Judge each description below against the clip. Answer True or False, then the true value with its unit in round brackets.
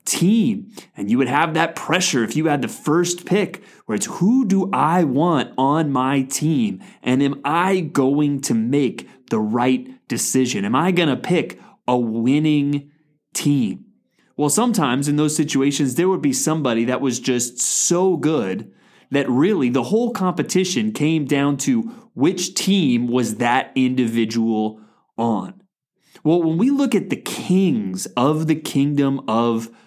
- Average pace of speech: True (155 wpm)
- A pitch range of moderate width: False (6.1 semitones)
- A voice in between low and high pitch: True (150 Hz)